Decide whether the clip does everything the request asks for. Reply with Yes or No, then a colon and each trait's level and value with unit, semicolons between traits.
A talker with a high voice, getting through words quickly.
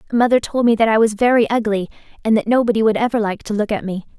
Yes: high, 220 Hz; fast, 260 wpm